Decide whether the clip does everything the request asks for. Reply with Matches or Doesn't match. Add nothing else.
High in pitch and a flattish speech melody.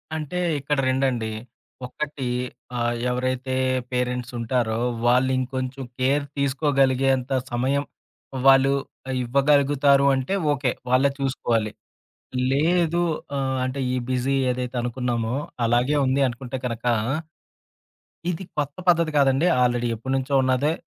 Doesn't match